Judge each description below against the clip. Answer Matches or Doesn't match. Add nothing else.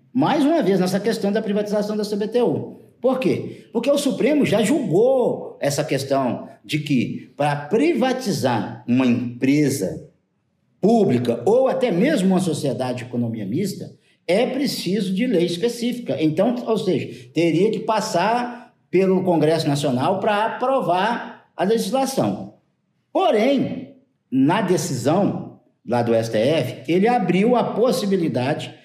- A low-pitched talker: Doesn't match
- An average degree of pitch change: Doesn't match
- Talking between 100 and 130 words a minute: Matches